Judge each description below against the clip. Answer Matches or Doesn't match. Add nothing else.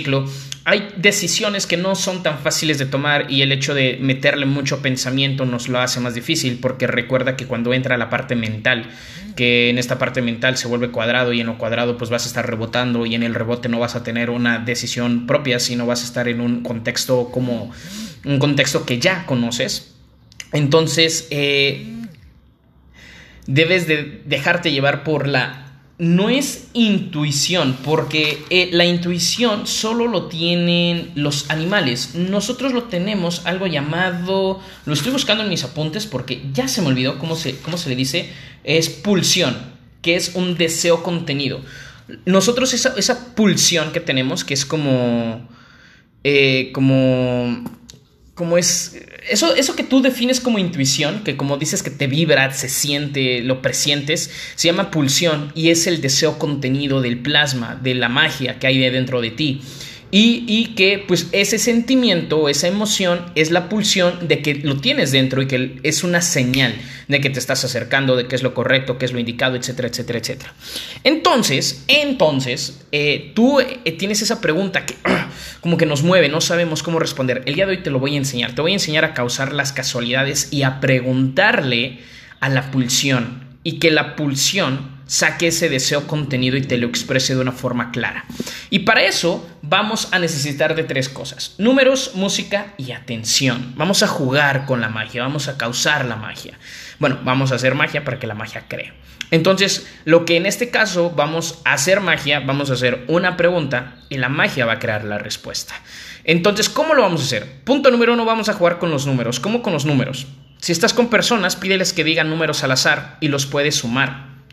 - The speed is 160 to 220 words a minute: Matches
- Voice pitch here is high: Doesn't match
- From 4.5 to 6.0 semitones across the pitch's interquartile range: Matches